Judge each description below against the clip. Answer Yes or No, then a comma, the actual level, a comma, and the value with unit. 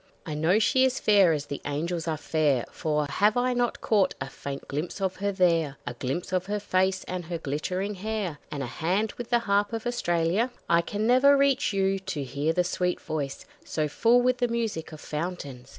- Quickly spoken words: Yes, fast, 210 wpm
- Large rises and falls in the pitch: Yes, wide, 5.7 semitones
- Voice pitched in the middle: Yes, medium, 180 Hz